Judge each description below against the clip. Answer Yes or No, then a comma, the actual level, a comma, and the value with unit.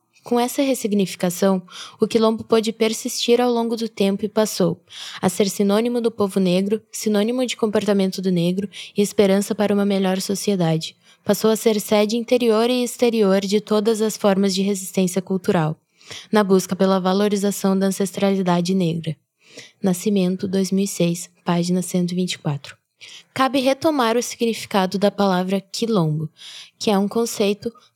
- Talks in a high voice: Yes, high, 200 Hz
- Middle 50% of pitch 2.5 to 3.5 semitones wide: Yes, average, 2.8 semitones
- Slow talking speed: No, average, 140 wpm